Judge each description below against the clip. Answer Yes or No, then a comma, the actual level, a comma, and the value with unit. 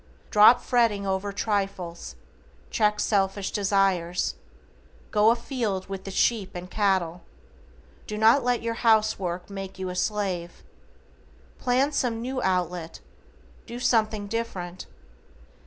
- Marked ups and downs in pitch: No, average, 3.4 semitones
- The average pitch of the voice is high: Yes, high, 205 Hz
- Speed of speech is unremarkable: No, slow, 120 wpm